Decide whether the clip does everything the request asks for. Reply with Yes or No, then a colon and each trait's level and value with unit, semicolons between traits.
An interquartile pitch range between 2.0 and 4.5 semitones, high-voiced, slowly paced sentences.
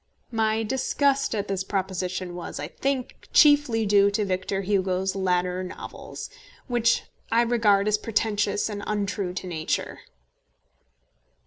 Yes: average, 3.3 semitones; high, 205 Hz; slow, 125 wpm